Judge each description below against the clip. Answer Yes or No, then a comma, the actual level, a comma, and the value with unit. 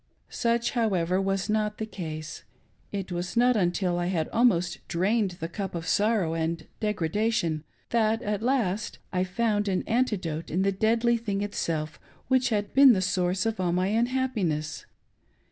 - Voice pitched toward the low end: No, high, 195 Hz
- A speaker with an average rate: Yes, average, 155 wpm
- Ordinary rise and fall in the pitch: Yes, average, 4.2 semitones